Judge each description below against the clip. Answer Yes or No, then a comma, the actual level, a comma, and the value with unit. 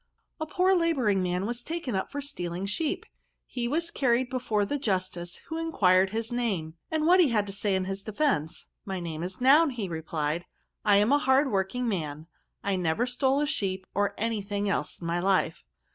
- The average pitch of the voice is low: No, high, 205 Hz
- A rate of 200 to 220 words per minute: Yes, fast, 205 wpm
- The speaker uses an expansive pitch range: Yes, wide, 6.2 semitones